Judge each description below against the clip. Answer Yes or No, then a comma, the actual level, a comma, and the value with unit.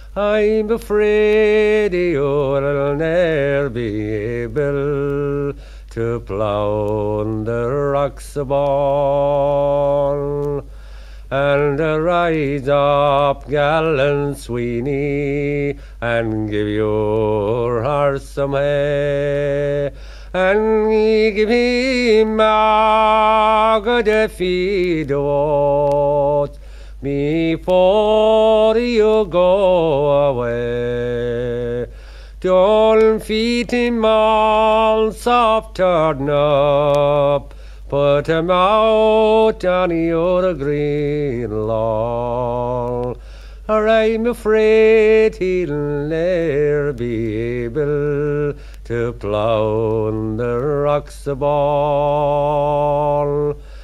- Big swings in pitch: Yes, wide, 6.2 semitones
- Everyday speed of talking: No, slow, 65 wpm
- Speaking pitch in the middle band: Yes, medium, 145 Hz